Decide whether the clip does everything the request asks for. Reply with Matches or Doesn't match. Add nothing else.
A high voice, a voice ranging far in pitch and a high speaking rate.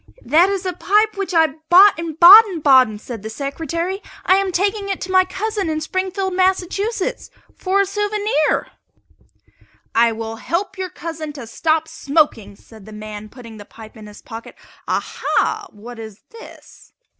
Doesn't match